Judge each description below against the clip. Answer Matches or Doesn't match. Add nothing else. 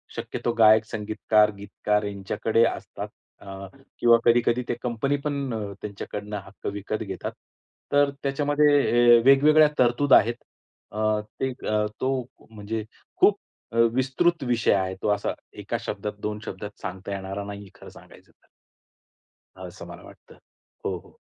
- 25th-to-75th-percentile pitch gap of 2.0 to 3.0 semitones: Doesn't match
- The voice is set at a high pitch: Doesn't match